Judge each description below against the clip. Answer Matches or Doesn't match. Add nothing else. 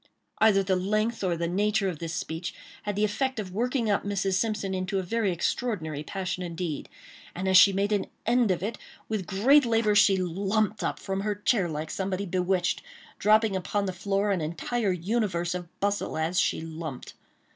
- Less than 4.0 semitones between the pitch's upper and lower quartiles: Matches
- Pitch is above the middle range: Matches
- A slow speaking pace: Doesn't match